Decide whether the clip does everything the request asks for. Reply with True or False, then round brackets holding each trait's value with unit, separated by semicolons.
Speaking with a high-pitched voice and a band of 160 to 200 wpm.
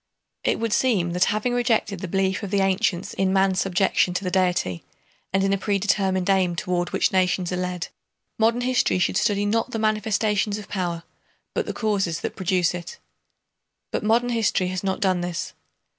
True (195 Hz; 185 wpm)